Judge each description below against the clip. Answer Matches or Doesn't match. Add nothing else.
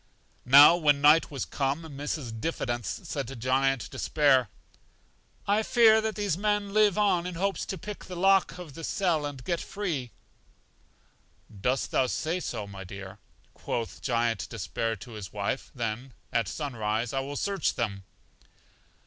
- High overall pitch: Doesn't match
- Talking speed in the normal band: Matches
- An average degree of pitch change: Doesn't match